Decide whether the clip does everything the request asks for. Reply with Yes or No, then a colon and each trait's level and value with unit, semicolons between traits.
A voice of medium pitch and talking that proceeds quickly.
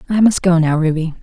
Yes: medium, 170 Hz; fast, 245 wpm